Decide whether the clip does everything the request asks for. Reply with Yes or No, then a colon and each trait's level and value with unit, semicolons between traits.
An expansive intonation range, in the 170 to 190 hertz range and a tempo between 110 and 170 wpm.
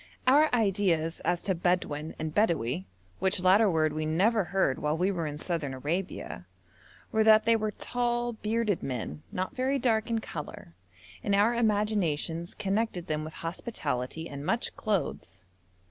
Yes: wide, 5.8 semitones; medium, 185 Hz; average, 155 wpm